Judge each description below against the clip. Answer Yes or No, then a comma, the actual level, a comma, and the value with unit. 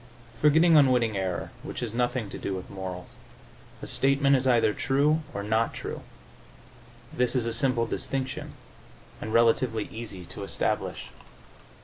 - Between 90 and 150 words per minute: Yes, average, 140 wpm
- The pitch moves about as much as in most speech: Yes, average, 4.0 semitones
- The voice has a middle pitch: No, low, 120 Hz